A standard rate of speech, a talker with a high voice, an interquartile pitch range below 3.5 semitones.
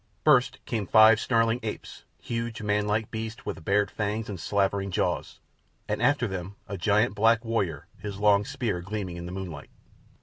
No: average, 165 wpm; low, 105 Hz; narrow, 2.5 semitones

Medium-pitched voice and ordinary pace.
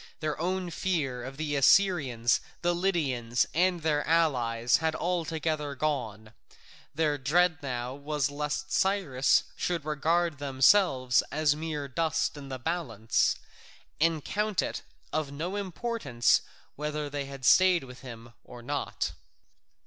No: medium, 150 Hz; slow, 125 wpm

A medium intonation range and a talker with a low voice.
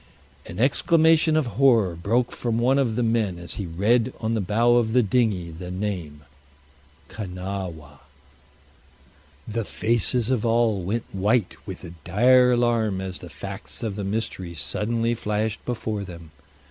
Yes: average, 4.2 semitones; low, 110 Hz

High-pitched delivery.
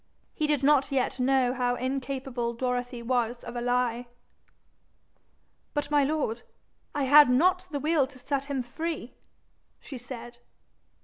Yes: very high, 260 Hz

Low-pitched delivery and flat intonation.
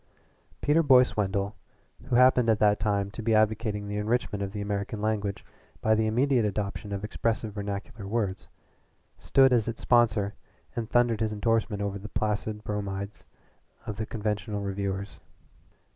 Yes: low, 105 Hz; narrow, 1.9 semitones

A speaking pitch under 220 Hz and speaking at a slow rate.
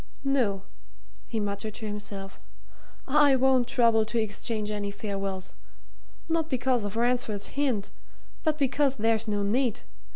No: high, 225 Hz; slow, 130 wpm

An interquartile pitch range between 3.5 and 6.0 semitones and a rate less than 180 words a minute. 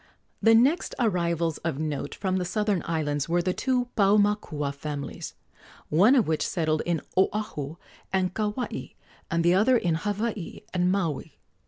Yes: average, 4.8 semitones; average, 150 wpm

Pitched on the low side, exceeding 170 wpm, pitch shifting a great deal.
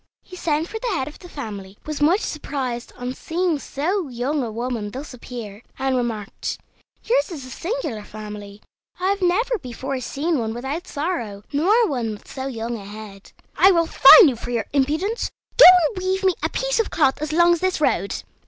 No: very high, 280 Hz; average, 200 wpm; wide, 7.3 semitones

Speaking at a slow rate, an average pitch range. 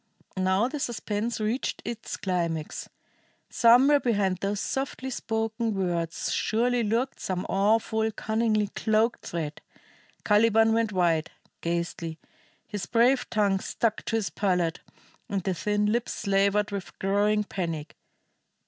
Yes: slow, 120 wpm; average, 3.2 semitones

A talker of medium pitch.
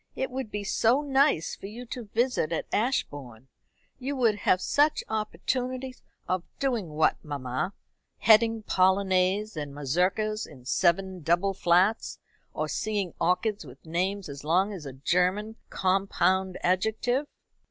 No: high, 195 Hz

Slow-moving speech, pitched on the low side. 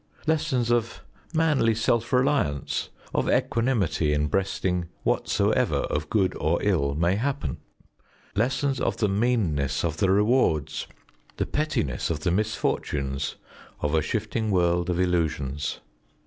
Yes: slow, 125 wpm; very low, 95 Hz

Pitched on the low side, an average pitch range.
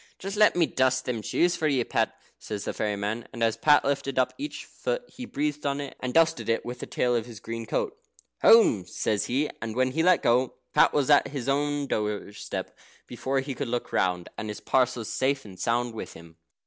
Yes: low, 130 Hz; average, 4.2 semitones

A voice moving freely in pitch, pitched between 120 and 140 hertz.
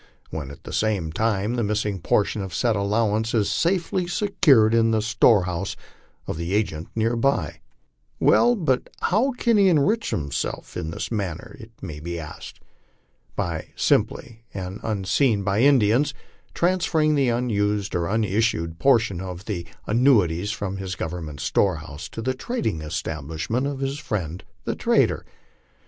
No: wide, 6.3 semitones; low, 105 Hz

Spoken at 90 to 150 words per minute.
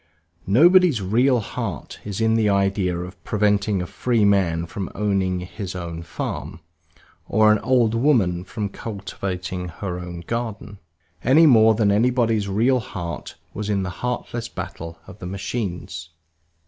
Yes: average, 145 wpm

